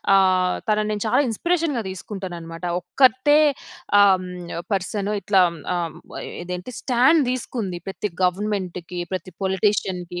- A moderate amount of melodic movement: Yes, average, 3.0 semitones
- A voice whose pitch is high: Yes, high, 195 Hz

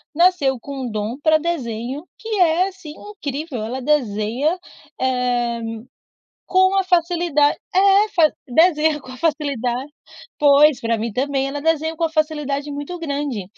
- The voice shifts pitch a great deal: No, average, 4.8 semitones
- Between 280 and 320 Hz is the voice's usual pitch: Yes, very high, 290 Hz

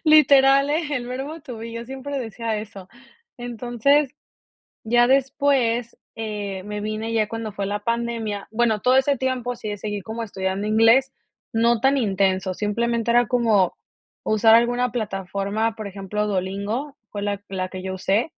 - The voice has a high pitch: Yes, high, 225 Hz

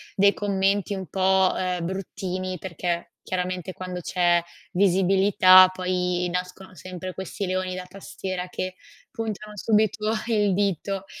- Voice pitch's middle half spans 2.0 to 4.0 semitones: No, narrow, 1.3 semitones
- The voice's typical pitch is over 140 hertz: Yes, medium, 185 Hz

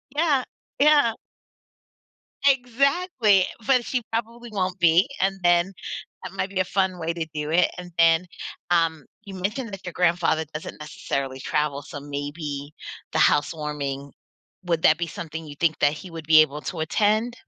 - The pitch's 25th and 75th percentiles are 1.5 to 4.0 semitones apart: No, average, 5.2 semitones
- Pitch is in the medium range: Yes, medium, 170 Hz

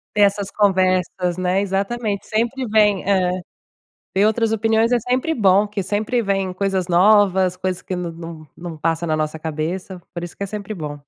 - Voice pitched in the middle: No, high, 195 Hz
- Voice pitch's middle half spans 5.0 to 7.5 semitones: No, average, 2.9 semitones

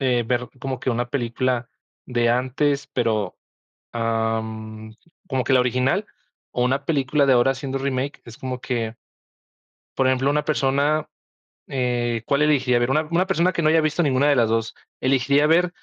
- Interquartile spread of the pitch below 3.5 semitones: Yes, average, 2.9 semitones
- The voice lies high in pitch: No, low, 130 Hz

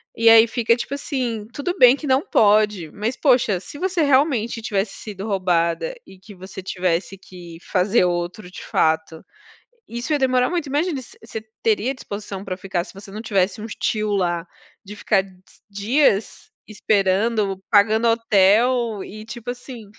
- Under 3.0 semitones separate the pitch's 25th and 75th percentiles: No, average, 4.2 semitones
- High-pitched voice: Yes, high, 215 Hz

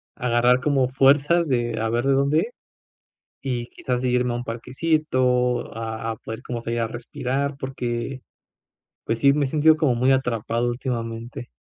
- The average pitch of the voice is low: Yes, low, 125 Hz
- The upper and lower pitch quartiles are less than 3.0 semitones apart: Yes, narrow, 2.5 semitones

